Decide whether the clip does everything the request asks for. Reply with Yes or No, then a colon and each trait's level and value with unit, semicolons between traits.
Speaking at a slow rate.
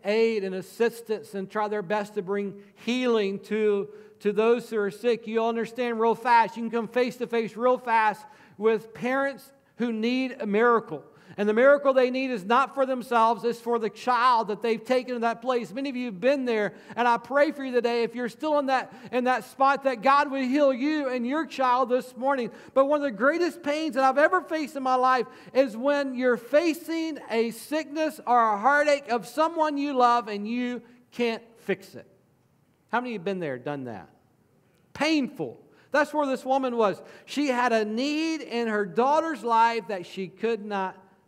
No: fast, 205 wpm